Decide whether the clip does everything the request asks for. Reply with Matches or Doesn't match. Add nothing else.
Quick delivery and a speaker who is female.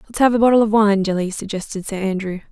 Matches